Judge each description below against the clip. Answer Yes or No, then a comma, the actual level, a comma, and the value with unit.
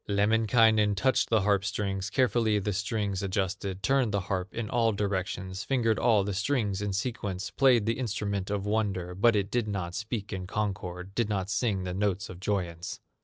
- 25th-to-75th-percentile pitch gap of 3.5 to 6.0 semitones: No, narrow, 2.6 semitones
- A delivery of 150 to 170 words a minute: No, average, 180 wpm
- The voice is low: Yes, low, 100 Hz